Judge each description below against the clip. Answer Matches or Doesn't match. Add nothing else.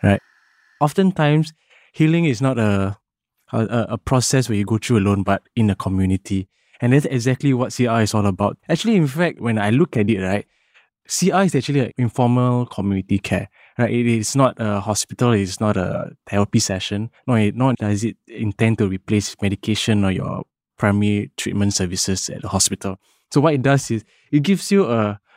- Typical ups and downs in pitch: Matches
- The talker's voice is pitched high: Doesn't match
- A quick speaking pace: Doesn't match